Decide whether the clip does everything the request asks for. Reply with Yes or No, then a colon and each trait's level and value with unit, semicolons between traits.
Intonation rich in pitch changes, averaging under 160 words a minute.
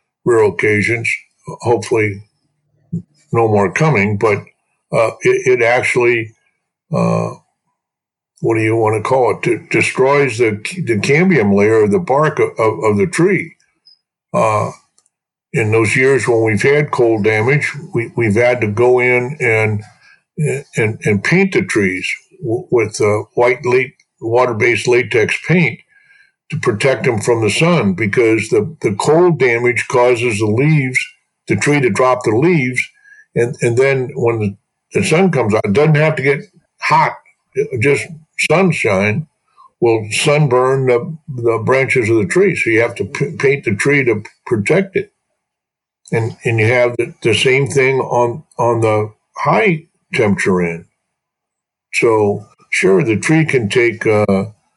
Yes: wide, 6.8 semitones; average, 150 wpm